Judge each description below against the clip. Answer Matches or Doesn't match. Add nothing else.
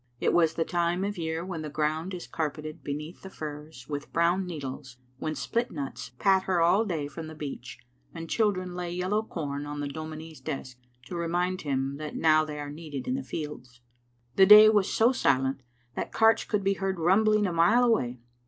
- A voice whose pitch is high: Doesn't match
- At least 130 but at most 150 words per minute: Doesn't match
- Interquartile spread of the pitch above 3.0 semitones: Matches